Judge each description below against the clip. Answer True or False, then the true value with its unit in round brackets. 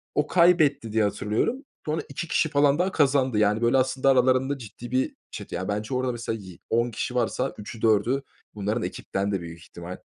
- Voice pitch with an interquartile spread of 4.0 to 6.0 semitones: True (4.6 semitones)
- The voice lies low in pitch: True (120 Hz)